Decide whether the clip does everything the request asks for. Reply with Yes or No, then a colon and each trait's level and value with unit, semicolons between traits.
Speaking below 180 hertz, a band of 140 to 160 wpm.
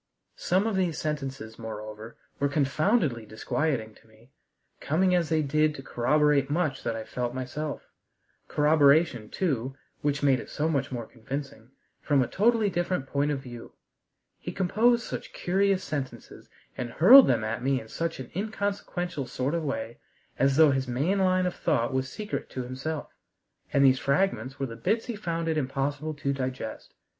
No: medium, 140 Hz; average, 170 wpm